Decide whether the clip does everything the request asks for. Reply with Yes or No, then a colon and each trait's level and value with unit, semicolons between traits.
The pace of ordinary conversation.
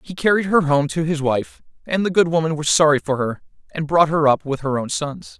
No: fast, 255 wpm